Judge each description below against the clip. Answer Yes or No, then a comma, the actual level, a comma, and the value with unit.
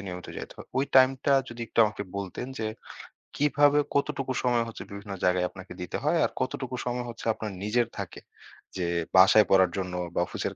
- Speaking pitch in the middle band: No, low, 115 Hz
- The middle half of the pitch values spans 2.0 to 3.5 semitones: No, wide, 5.5 semitones